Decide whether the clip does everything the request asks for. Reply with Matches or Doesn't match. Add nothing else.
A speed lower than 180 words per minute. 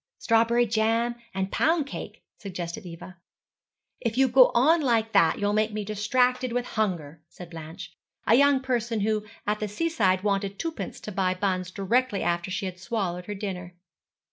Matches